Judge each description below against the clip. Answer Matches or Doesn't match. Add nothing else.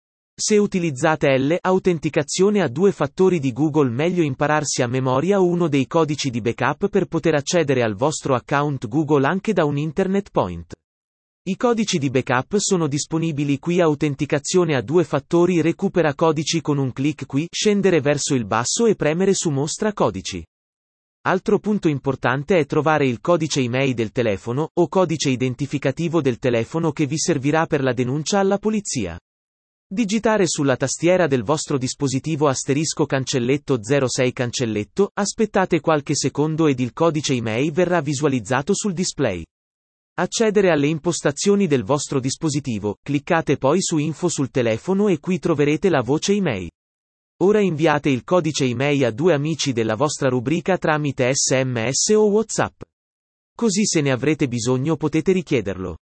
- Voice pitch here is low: Doesn't match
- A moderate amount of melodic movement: Matches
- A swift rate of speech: Doesn't match